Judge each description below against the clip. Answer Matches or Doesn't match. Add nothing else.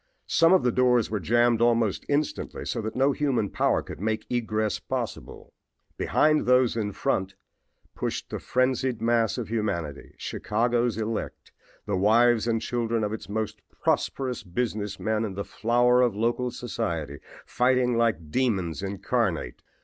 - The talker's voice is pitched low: Matches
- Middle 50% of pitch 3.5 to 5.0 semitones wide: Doesn't match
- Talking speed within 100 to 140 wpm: Doesn't match